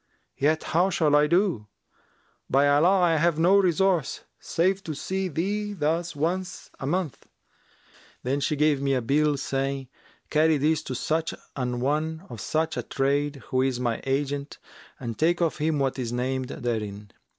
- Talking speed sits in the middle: Yes, average, 165 wpm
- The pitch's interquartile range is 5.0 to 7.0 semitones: No, average, 3.7 semitones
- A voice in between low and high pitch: Yes, medium, 150 Hz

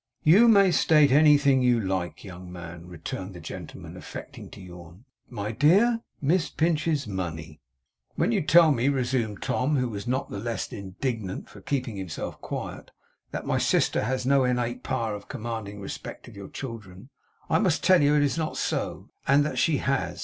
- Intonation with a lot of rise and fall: Yes, wide, 6.8 semitones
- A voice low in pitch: Yes, low, 125 Hz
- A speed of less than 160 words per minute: No, average, 180 wpm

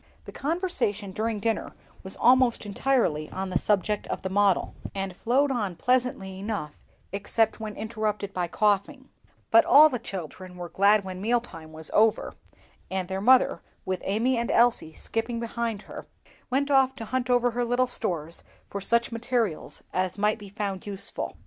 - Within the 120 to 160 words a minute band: No, average, 170 wpm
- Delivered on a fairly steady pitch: No, average, 4.1 semitones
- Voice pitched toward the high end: Yes, high, 215 Hz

